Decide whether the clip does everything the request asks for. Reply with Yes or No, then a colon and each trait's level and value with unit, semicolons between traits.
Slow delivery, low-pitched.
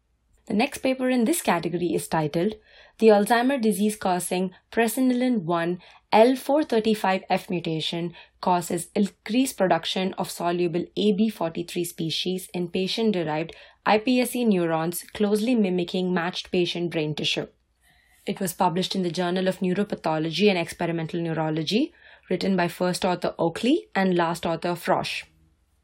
No: slow, 120 wpm; medium, 185 Hz